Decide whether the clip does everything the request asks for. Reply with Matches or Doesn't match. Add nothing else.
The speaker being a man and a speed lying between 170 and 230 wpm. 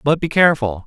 Matches